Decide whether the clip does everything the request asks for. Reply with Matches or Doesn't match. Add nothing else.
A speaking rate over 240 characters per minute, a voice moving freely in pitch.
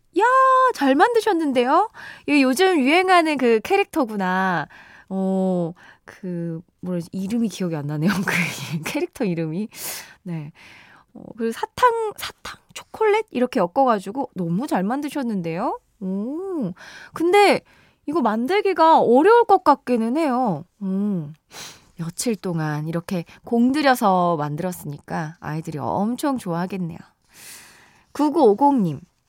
Matches